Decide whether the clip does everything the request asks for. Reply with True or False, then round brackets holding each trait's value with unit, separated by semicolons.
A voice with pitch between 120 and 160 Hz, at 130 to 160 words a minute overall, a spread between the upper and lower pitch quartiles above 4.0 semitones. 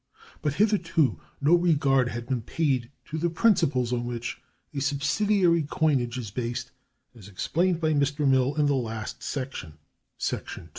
True (140 Hz; 155 wpm; 4.5 semitones)